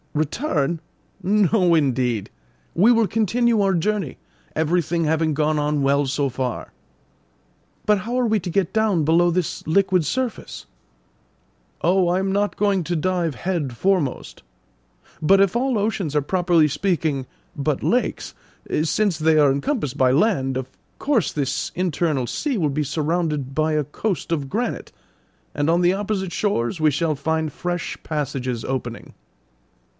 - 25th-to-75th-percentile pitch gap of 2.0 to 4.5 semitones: No, average, 5.0 semitones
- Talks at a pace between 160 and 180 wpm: No, average, 150 wpm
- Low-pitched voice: No, medium, 165 Hz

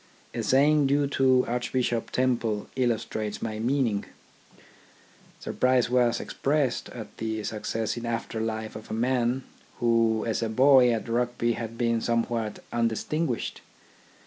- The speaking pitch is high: No, low, 120 Hz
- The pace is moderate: No, slow, 130 wpm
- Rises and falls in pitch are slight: Yes, narrow, 2.2 semitones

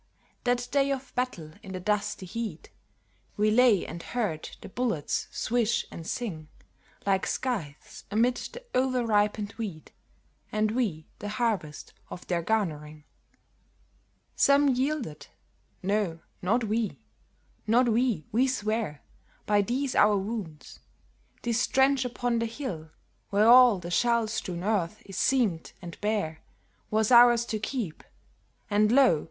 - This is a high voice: Yes, high, 215 Hz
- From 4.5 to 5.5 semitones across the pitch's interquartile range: Yes, average, 4.9 semitones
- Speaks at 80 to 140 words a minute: Yes, slow, 135 wpm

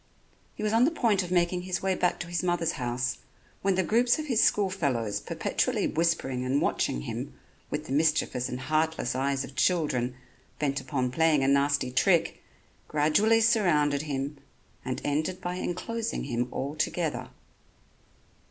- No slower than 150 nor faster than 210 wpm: Yes, average, 160 wpm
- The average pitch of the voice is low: No, medium, 155 Hz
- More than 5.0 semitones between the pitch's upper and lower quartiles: Yes, wide, 5.4 semitones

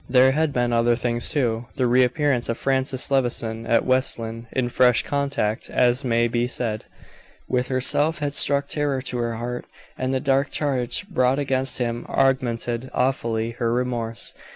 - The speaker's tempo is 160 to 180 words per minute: Yes, average, 170 wpm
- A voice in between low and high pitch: No, low, 125 Hz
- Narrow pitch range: Yes, narrow, 2.2 semitones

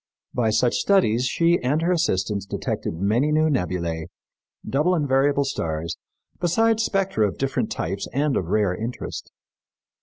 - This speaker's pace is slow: No, average, 145 wpm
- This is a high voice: No, low, 130 Hz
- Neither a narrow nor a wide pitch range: No, wide, 7.9 semitones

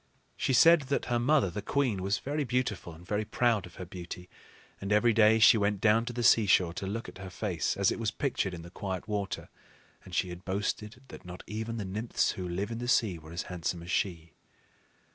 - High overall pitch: No, low, 105 Hz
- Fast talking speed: Yes, fast, 225 wpm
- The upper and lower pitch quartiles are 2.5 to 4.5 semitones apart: Yes, average, 4.2 semitones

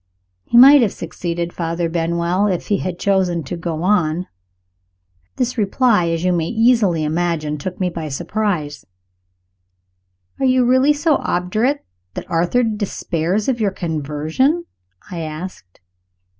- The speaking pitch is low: No, medium, 180 Hz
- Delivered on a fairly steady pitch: No, average, 5.1 semitones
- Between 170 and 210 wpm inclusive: No, slow, 135 wpm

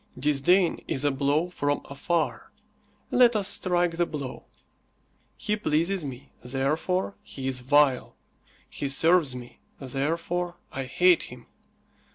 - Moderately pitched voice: Yes, medium, 150 Hz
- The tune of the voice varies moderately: Yes, average, 4.7 semitones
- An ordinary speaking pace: No, slow, 125 wpm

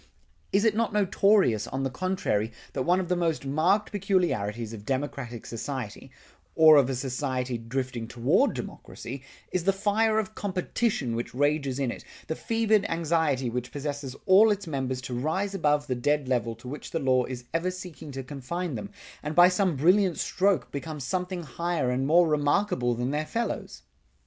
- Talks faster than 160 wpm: Yes, average, 175 wpm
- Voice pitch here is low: No, medium, 150 Hz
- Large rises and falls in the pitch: Yes, wide, 6.3 semitones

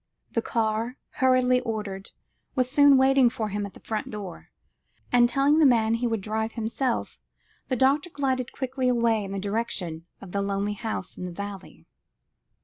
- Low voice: No, high, 230 Hz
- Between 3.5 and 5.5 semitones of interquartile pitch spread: Yes, average, 3.9 semitones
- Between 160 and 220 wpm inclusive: Yes, average, 170 wpm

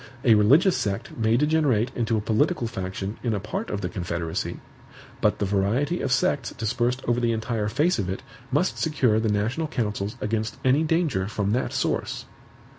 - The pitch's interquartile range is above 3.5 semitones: Yes, average, 4.3 semitones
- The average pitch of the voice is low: Yes, low, 115 Hz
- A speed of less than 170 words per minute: No, average, 180 wpm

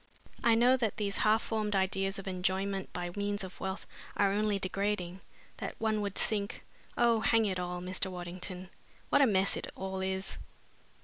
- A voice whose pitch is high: Yes, high, 195 Hz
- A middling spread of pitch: No, narrow, 2.1 semitones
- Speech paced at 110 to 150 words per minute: No, average, 175 wpm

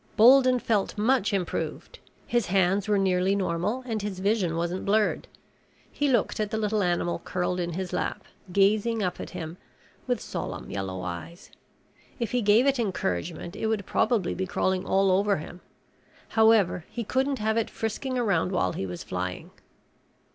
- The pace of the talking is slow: No, average, 165 wpm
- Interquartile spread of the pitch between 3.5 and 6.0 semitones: Yes, average, 3.8 semitones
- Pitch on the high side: Yes, high, 200 Hz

